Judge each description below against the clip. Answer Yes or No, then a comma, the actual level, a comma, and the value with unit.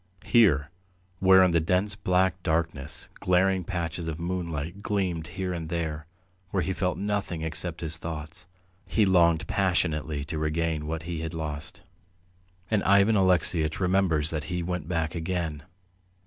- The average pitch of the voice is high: No, very low, 85 Hz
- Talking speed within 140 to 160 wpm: Yes, average, 150 wpm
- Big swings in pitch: No, average, 2.8 semitones